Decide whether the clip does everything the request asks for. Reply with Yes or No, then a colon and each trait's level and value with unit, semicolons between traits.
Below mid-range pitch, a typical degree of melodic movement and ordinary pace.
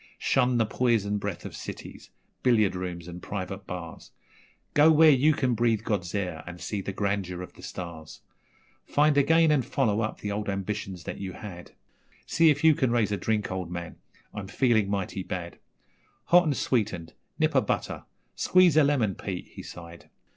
No: low, 105 Hz; wide, 5.7 semitones; average, 180 wpm